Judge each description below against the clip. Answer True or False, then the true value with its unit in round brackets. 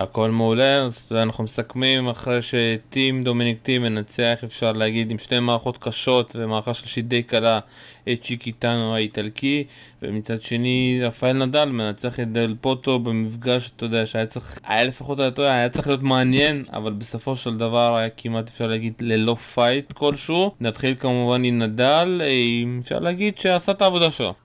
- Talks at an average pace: False (165 wpm)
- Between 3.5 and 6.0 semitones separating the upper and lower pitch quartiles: False (2.5 semitones)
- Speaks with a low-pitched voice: True (120 Hz)